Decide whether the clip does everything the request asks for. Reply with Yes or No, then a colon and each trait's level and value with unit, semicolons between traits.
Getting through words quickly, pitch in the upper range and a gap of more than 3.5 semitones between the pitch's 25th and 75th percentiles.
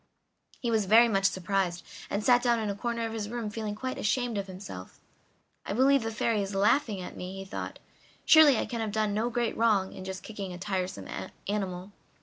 No: fast, 210 wpm; high, 210 Hz; average, 3.2 semitones